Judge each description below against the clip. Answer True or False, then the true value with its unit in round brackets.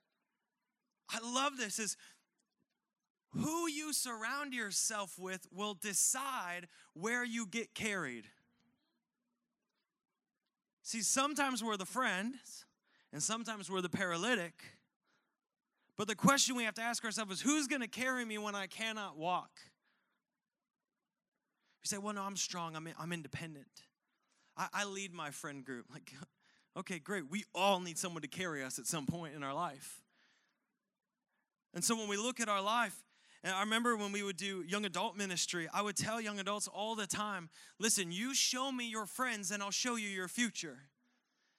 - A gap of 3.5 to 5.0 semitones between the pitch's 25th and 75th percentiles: True (4.7 semitones)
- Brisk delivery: False (165 wpm)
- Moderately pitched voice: False (210 Hz)